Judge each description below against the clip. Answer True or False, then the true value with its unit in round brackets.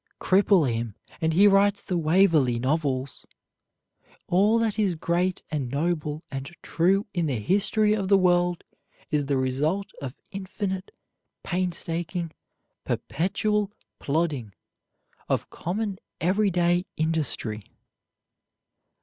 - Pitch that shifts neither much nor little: True (4.8 semitones)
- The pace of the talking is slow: True (110 wpm)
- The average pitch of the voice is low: False (175 Hz)